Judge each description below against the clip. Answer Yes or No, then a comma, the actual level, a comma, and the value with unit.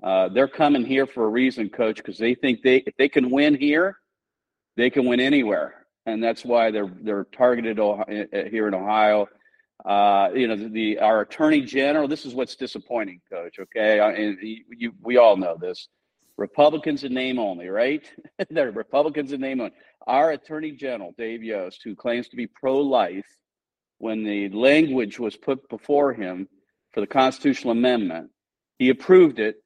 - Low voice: Yes, low, 130 Hz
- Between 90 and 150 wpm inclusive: No, average, 180 wpm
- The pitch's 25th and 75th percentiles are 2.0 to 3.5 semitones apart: No, average, 5.0 semitones